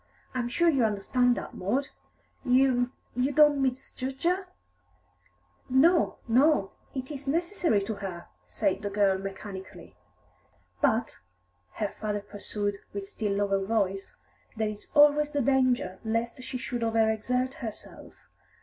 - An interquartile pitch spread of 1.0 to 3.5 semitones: No, average, 4.8 semitones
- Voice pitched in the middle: No, high, 240 Hz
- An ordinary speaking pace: No, slow, 130 wpm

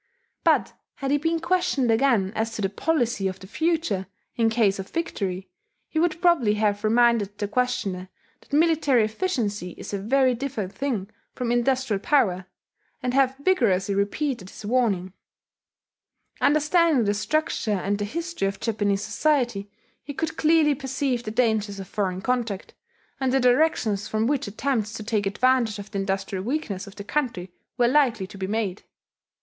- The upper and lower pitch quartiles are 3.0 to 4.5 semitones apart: No, wide, 5.4 semitones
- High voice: Yes, high, 225 Hz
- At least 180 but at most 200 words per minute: No, average, 165 wpm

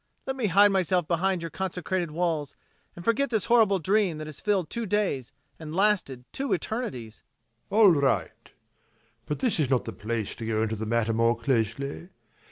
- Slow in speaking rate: No, average, 180 wpm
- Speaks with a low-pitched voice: No, medium, 170 Hz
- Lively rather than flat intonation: Yes, wide, 8.4 semitones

